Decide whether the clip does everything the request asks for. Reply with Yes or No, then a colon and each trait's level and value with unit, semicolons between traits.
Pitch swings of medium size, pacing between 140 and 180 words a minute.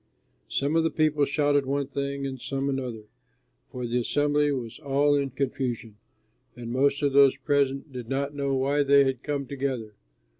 No: narrow, 1.6 semitones; average, 175 wpm